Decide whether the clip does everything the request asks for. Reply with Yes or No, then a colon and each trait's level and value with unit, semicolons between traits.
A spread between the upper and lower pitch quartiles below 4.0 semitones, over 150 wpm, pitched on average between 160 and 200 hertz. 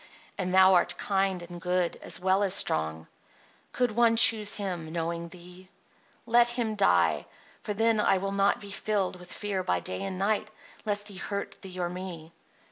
Yes: narrow, 2.6 semitones; average, 180 wpm; high, 190 Hz